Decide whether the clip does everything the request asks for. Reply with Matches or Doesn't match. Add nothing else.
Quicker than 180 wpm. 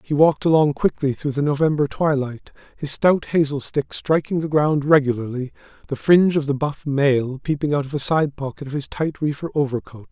Matches